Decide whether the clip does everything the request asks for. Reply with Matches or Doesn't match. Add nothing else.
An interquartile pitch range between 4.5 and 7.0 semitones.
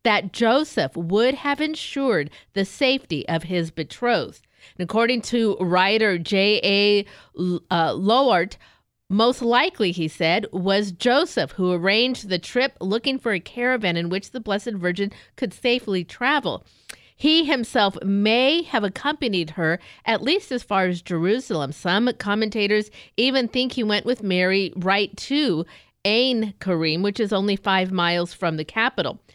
Matches